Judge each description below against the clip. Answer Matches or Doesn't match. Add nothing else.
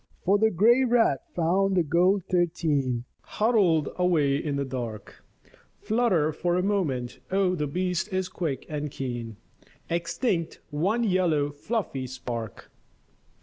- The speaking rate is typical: Doesn't match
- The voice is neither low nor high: Matches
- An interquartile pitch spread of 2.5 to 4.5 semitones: Doesn't match